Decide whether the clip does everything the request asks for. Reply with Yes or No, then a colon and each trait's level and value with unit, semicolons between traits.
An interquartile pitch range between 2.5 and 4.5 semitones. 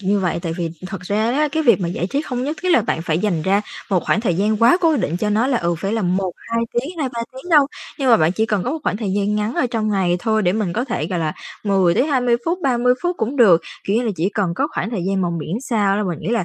No: average, 5.2 semitones